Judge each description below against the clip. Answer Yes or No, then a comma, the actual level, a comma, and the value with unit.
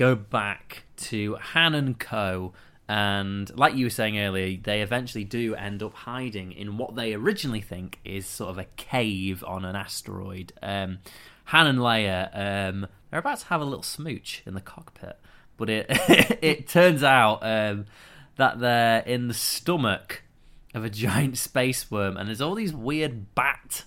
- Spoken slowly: No, average, 170 wpm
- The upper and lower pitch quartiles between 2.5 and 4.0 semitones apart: No, average, 4.6 semitones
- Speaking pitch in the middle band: No, low, 110 Hz